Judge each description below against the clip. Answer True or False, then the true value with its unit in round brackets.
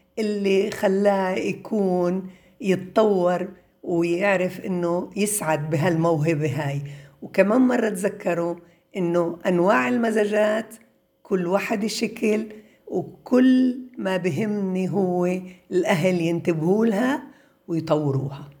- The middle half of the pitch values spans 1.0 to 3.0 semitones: False (3.6 semitones)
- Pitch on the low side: False (185 Hz)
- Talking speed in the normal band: True (85 wpm)